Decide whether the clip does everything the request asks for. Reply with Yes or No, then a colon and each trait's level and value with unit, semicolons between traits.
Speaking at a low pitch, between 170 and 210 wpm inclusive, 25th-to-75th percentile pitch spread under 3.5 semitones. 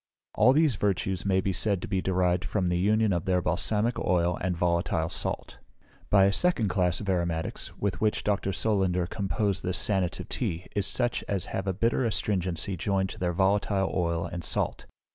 Yes: very low, 95 Hz; average, 185 wpm; narrow, 2.5 semitones